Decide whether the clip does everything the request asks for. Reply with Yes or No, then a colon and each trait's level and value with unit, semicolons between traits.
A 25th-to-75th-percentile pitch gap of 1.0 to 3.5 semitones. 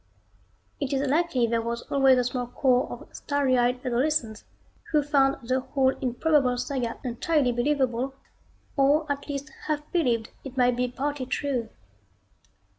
Yes: narrow, 2.6 semitones